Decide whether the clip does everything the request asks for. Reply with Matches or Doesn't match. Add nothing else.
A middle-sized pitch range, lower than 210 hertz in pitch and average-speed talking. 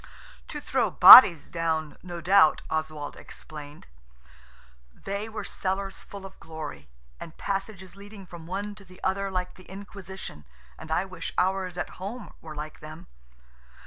Matches